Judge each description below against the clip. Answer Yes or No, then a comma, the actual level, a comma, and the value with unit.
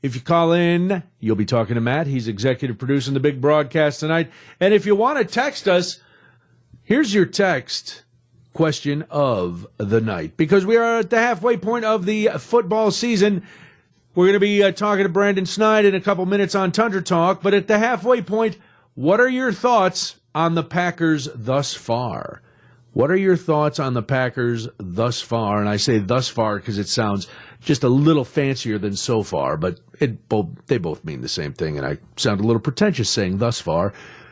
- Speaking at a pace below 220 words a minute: Yes, average, 200 wpm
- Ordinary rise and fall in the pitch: No, wide, 8.9 semitones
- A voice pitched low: No, medium, 155 Hz